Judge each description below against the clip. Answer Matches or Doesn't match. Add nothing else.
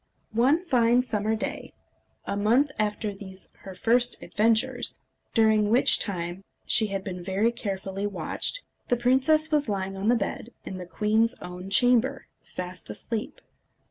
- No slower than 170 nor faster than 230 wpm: Doesn't match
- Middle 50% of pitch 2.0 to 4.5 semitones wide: Matches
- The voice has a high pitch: Matches